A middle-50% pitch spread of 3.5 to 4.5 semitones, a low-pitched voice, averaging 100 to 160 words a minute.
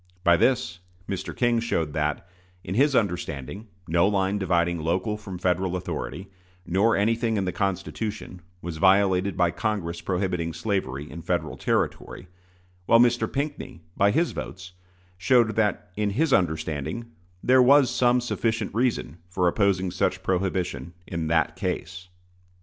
Yes: average, 4.2 semitones; very low, 95 Hz; average, 140 wpm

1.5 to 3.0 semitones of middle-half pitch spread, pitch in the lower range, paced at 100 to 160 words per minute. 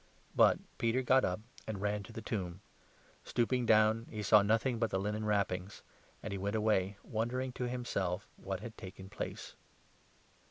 No: average, 2.7 semitones; low, 105 Hz; average, 175 wpm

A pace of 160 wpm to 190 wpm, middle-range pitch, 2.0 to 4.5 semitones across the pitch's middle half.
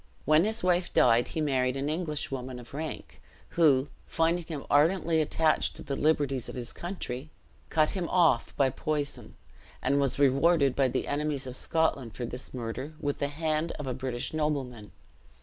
Yes: average, 170 wpm; medium, 145 Hz; average, 3.5 semitones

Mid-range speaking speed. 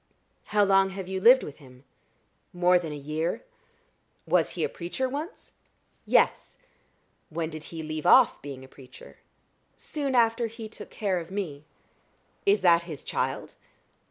Yes: average, 155 wpm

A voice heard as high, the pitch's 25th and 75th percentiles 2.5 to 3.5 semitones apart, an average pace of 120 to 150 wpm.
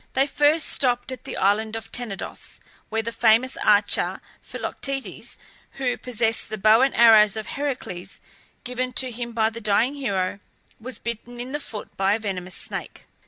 No: high, 230 Hz; average, 3.0 semitones; average, 165 wpm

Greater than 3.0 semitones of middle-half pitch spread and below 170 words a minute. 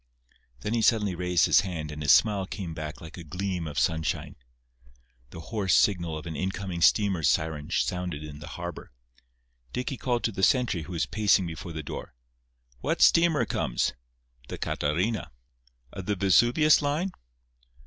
Yes: average, 4.8 semitones; average, 160 wpm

